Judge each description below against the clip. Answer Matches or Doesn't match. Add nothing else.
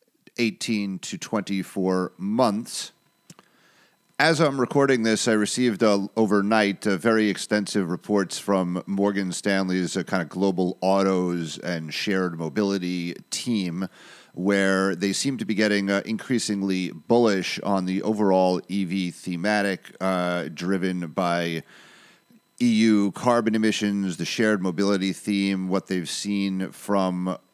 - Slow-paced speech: Matches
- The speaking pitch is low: Matches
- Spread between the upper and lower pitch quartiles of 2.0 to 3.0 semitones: Matches